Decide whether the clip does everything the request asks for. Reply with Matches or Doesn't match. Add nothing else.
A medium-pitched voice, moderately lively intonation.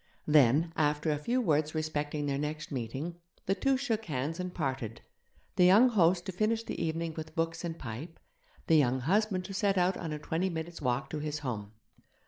Matches